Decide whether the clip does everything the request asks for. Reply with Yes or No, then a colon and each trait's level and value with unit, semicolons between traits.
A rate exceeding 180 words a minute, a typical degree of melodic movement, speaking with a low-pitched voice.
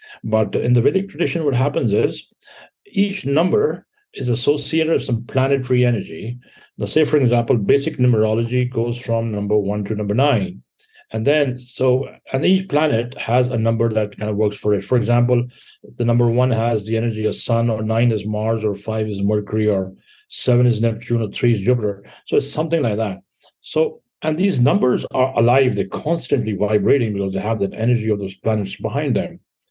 Yes: average, 190 wpm; average, 3.7 semitones; low, 115 Hz